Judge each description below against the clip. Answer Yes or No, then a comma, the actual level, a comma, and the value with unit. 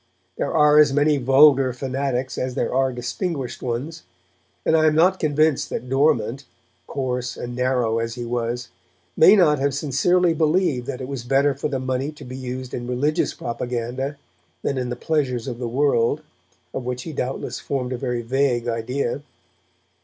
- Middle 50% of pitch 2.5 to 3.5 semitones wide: Yes, average, 2.9 semitones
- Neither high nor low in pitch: No, low, 130 Hz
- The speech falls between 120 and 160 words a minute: No, average, 175 wpm